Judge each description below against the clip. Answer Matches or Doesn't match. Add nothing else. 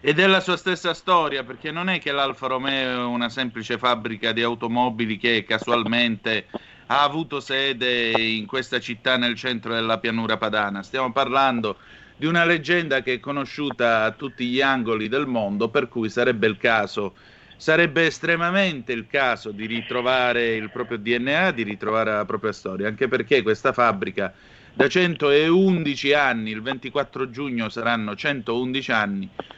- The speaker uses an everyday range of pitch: Matches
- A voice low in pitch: Matches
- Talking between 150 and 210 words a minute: Matches